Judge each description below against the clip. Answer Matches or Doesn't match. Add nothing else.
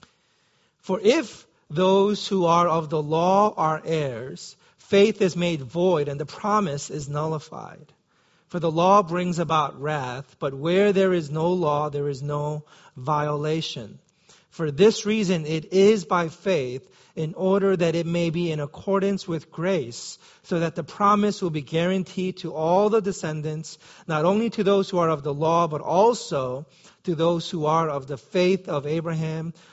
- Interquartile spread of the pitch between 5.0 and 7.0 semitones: Doesn't match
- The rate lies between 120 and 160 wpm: Doesn't match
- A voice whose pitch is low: Doesn't match